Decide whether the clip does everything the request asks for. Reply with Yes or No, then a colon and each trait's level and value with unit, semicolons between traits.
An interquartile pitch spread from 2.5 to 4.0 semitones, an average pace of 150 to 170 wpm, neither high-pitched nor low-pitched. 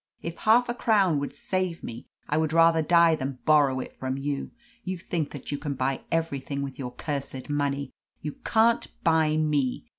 No: average, 3.2 semitones; average, 185 wpm; medium, 150 Hz